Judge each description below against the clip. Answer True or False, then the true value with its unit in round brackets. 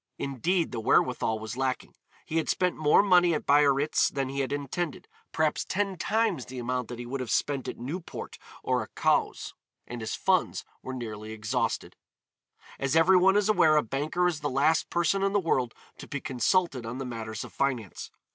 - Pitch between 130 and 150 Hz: True (140 Hz)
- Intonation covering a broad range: True (5.7 semitones)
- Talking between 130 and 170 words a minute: False (190 wpm)